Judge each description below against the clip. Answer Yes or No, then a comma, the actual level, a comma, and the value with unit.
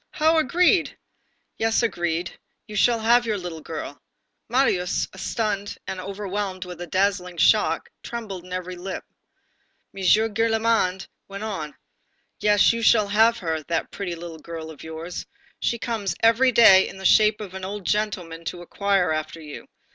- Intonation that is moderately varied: Yes, average, 4.0 semitones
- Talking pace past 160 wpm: No, average, 155 wpm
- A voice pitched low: No, high, 195 Hz